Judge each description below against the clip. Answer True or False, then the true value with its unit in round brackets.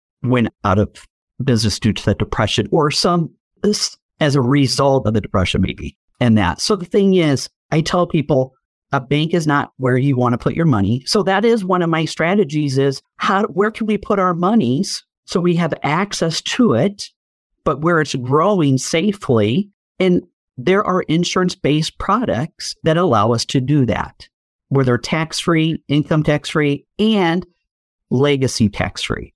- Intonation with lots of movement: True (5.7 semitones)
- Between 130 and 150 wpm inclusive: False (175 wpm)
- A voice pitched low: False (155 Hz)